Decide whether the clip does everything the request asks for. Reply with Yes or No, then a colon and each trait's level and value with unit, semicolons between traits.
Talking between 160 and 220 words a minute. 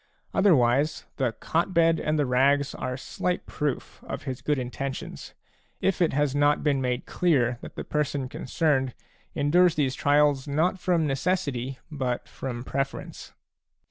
No: average, 145 wpm